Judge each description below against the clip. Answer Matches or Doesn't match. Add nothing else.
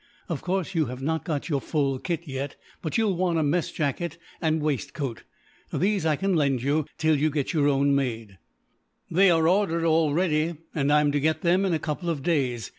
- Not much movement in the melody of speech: Doesn't match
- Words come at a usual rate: Doesn't match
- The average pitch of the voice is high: Doesn't match